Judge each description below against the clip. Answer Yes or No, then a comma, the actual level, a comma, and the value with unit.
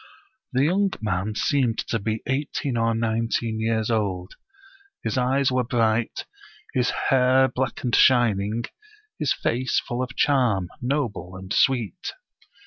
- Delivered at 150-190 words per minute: No, slow, 135 wpm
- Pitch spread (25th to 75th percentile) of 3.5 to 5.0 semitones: No, average, 2.9 semitones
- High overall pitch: No, low, 120 Hz